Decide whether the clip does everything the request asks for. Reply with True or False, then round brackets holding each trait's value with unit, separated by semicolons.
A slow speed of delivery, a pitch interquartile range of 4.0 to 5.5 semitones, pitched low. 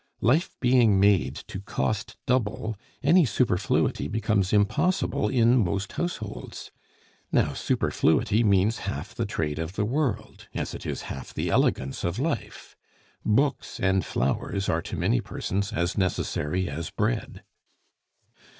True (130 wpm; 4.5 semitones; 100 Hz)